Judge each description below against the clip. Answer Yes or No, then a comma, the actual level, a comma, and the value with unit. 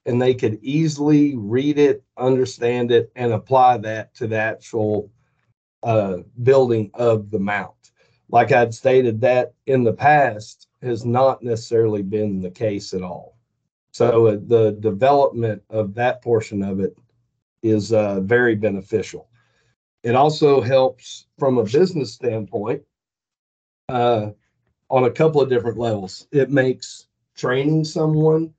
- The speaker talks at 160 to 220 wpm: No, slow, 135 wpm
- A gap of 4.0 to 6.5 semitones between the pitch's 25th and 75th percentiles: No, average, 3.3 semitones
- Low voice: Yes, low, 120 Hz